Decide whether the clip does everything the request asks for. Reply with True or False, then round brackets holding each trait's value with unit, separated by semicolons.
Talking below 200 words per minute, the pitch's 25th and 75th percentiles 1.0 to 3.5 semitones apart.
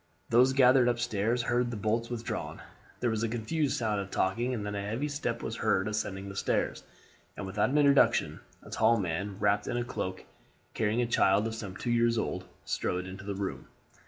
False (205 wpm; 3.2 semitones)